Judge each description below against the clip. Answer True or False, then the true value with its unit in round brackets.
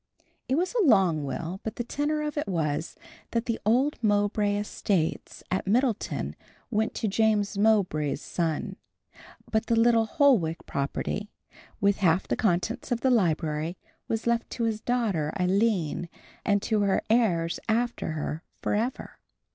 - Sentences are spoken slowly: False (145 wpm)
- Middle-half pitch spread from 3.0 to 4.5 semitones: False (5.0 semitones)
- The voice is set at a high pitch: True (210 Hz)